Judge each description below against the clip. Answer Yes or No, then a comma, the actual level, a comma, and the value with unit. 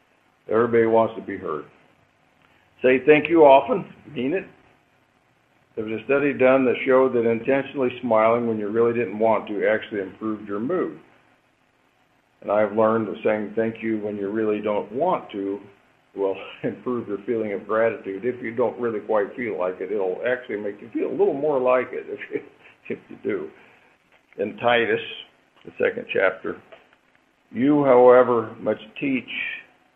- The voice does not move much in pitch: No, average, 4.6 semitones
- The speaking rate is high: No, average, 165 wpm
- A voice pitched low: Yes, low, 115 Hz